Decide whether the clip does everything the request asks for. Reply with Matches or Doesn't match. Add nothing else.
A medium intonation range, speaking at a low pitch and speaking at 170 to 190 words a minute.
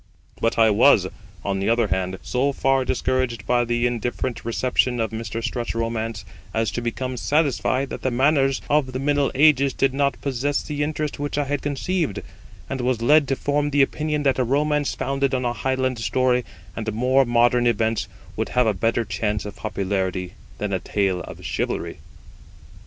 Matches